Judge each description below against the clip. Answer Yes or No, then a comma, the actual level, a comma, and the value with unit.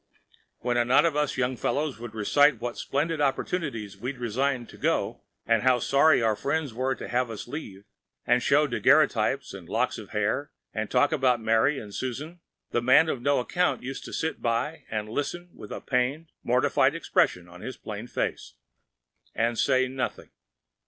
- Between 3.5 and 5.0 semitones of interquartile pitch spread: Yes, average, 3.8 semitones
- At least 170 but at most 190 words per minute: Yes, average, 180 wpm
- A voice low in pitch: Yes, low, 130 Hz